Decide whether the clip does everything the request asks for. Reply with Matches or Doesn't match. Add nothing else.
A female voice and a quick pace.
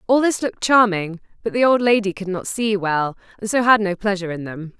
Matches